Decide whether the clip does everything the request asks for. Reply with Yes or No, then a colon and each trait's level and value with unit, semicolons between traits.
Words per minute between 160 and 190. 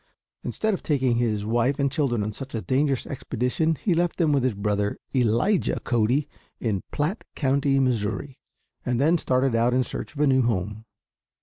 Yes: average, 180 wpm